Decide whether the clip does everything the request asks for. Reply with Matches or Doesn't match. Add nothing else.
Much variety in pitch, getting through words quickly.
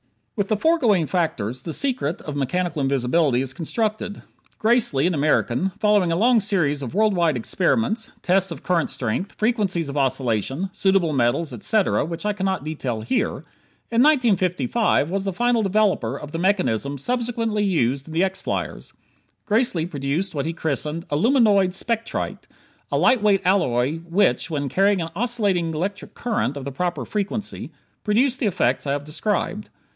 Doesn't match